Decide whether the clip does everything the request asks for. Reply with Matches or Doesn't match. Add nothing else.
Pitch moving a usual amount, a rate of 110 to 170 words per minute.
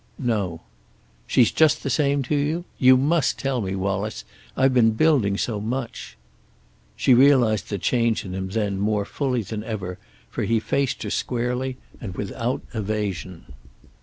Matches